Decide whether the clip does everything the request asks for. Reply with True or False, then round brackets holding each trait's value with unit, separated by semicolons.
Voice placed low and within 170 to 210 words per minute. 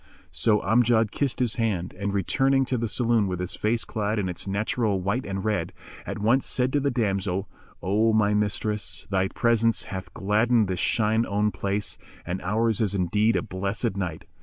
True (105 Hz; 185 wpm)